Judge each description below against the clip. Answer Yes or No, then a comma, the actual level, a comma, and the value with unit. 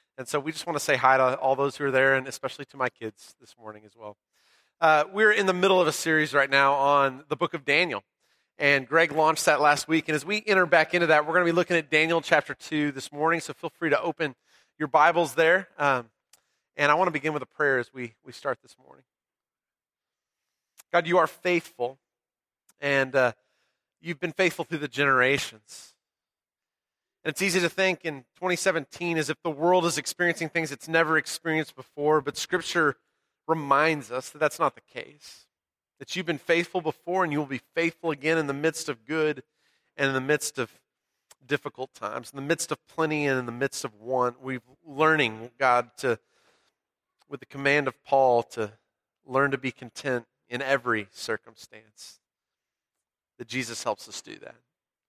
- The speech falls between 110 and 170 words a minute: No, average, 195 wpm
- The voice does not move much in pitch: No, average, 3.7 semitones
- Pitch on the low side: No, medium, 150 Hz